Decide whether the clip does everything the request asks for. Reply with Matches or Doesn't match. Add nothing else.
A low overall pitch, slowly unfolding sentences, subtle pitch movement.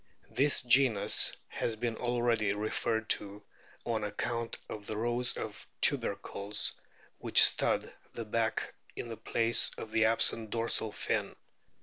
Matches